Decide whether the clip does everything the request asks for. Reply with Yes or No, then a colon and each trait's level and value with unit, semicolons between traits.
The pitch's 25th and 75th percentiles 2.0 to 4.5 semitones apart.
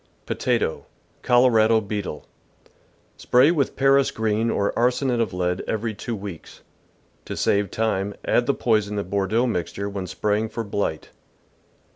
Yes: average, 3.0 semitones